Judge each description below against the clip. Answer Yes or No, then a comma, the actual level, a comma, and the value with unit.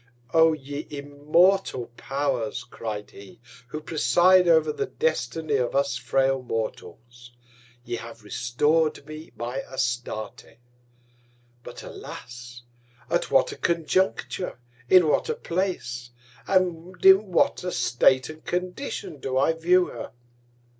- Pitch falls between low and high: Yes, medium, 145 Hz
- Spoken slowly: Yes, slow, 120 wpm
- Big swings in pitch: Yes, wide, 5.7 semitones